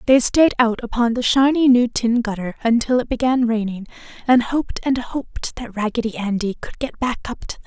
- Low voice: No, high, 240 Hz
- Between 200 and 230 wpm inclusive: Yes, fast, 205 wpm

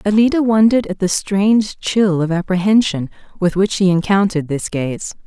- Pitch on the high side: Yes, high, 195 Hz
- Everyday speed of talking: Yes, average, 160 wpm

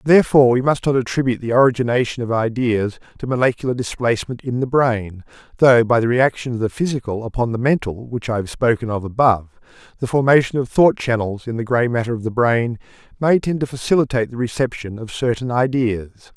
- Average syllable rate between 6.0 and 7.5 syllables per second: Yes, 6.1 syllables/s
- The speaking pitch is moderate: No, low, 120 Hz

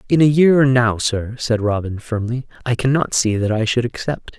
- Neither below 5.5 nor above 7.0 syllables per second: No, 5.0 syllables/s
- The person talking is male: Yes, male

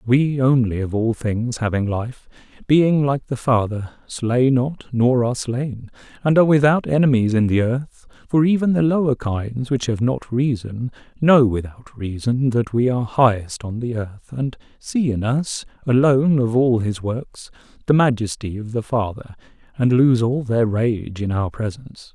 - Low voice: Yes, low, 125 Hz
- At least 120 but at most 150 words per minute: No, average, 175 wpm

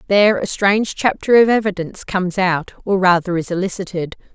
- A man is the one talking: No, female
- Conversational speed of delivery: Yes, average, 165 wpm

